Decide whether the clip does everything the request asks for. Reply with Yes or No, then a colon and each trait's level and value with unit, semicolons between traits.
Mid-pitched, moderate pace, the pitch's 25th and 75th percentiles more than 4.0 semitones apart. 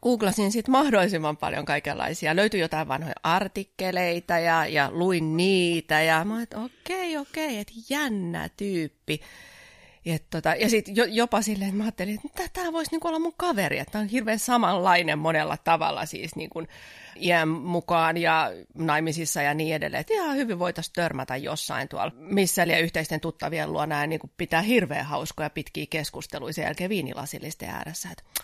No: medium, 175 Hz; fast, 165 wpm; average, 5.2 semitones